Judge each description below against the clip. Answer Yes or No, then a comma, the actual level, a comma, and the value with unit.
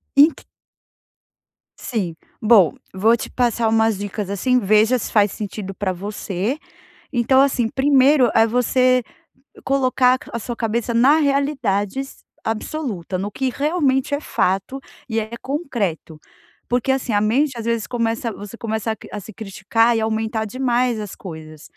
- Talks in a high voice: Yes, high, 230 Hz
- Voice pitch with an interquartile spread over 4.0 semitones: No, average, 3.7 semitones